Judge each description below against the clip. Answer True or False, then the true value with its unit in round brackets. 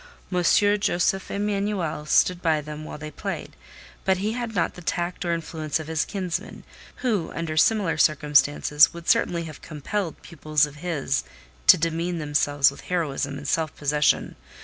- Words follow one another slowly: False (160 wpm)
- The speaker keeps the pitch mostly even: False (3.1 semitones)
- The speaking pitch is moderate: True (160 Hz)